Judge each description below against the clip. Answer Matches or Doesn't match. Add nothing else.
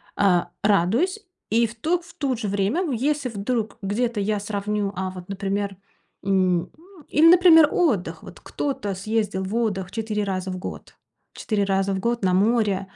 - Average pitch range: Matches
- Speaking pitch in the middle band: Doesn't match